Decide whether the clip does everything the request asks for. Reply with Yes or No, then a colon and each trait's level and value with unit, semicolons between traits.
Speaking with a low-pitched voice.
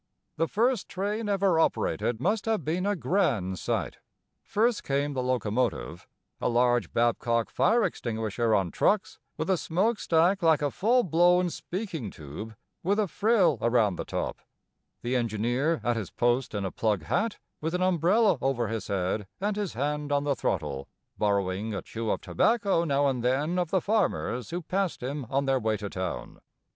No: medium, 145 Hz